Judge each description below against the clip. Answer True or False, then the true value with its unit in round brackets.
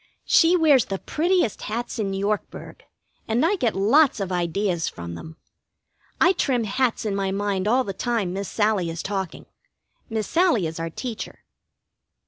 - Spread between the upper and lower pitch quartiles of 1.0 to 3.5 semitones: False (4.7 semitones)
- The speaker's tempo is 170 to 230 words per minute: False (160 wpm)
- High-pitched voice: True (210 Hz)